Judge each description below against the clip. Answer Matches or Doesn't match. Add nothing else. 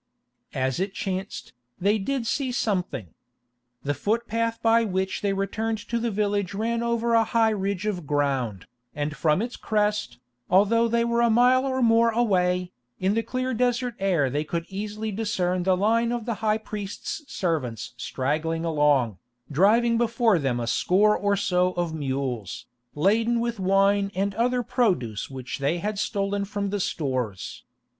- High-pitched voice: Matches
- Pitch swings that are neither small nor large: Doesn't match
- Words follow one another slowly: Doesn't match